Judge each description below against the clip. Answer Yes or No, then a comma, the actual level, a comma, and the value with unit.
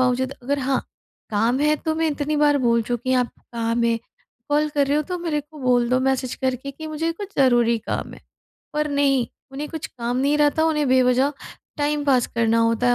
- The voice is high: Yes, very high, 275 Hz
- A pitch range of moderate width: Yes, average, 3.4 semitones